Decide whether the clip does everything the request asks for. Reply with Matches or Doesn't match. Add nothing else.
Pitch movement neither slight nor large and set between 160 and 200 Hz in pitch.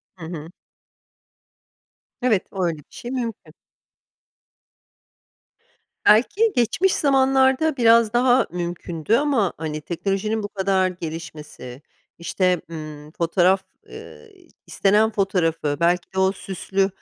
Doesn't match